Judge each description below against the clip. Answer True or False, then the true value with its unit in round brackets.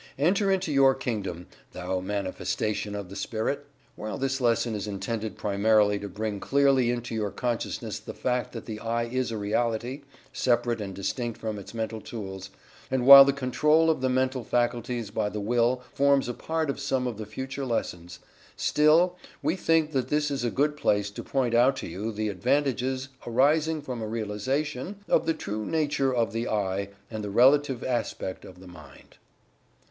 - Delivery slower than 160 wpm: False (180 wpm)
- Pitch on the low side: True (120 Hz)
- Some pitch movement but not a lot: True (4.5 semitones)